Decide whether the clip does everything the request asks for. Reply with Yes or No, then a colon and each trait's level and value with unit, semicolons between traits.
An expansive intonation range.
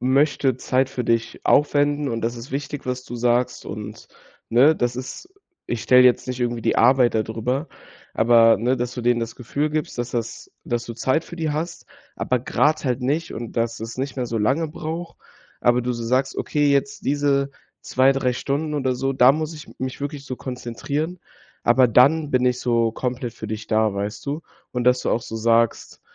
No: average, 3.2 semitones